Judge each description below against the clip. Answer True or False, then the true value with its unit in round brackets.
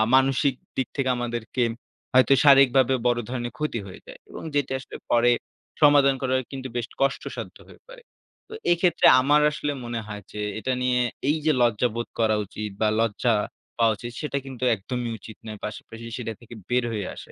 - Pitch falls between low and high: False (125 Hz)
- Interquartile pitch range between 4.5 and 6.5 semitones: False (2.9 semitones)